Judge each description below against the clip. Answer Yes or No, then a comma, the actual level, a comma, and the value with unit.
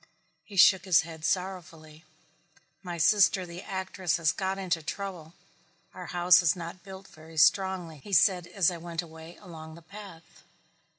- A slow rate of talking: No, average, 160 wpm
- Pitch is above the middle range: No, medium, 175 Hz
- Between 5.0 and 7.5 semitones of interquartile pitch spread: No, narrow, 2.6 semitones